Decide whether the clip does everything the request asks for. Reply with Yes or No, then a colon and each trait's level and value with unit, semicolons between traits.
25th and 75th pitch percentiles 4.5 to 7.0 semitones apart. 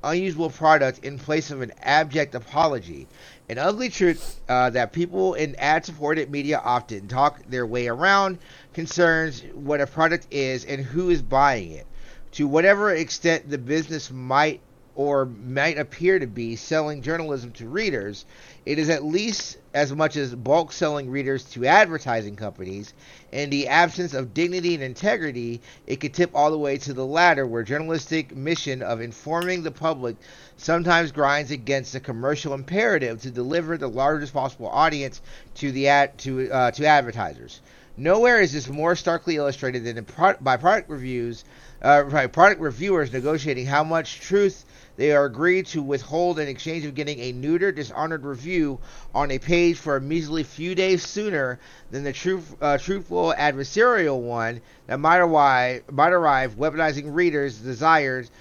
No: average, 3.9 semitones